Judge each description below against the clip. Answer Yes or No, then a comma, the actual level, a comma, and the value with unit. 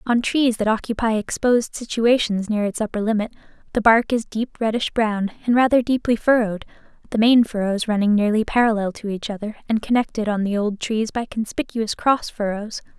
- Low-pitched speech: No, high, 220 Hz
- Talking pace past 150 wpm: Yes, average, 180 wpm